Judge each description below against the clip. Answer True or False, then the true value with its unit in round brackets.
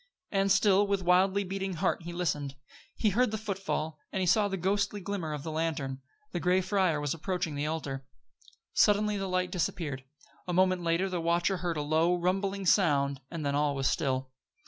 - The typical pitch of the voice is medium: True (180 Hz)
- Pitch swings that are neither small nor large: True (4.0 semitones)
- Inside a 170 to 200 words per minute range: True (190 wpm)